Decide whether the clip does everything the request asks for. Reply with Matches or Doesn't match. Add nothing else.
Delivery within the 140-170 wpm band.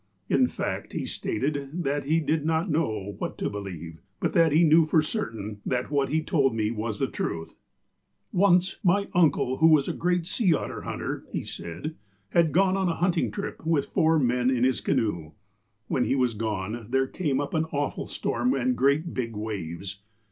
Doesn't match